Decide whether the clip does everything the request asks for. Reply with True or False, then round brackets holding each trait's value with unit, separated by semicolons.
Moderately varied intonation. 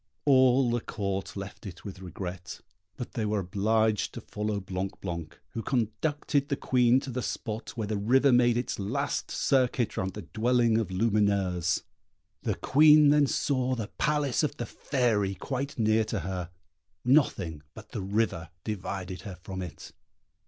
True (4.7 semitones)